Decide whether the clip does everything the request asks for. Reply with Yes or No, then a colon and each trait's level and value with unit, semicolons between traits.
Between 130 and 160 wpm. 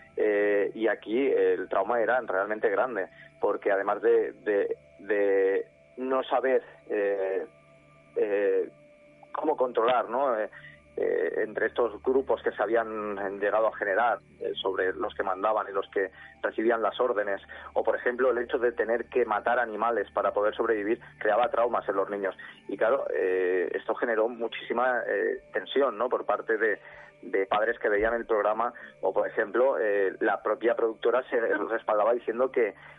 Yes: average, 155 wpm